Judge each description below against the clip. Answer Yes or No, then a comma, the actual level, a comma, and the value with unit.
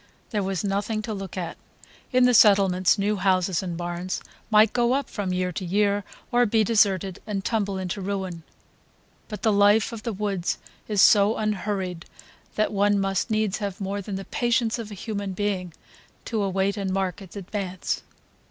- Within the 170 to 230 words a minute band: Yes, average, 180 wpm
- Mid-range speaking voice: No, high, 200 Hz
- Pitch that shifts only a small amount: Yes, narrow, 2.1 semitones